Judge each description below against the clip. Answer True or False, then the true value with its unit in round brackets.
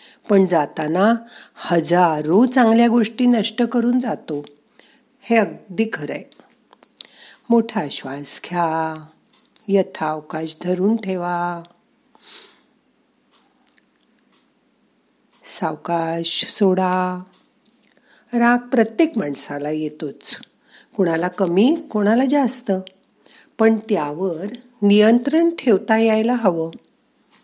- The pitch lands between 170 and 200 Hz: False (210 Hz)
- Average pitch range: False (5.7 semitones)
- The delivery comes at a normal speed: False (70 wpm)